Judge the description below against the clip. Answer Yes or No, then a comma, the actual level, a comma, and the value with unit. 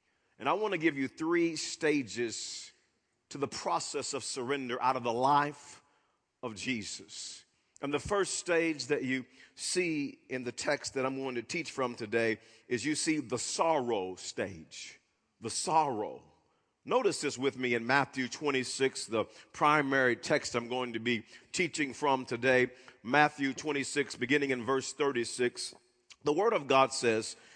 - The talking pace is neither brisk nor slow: Yes, average, 155 wpm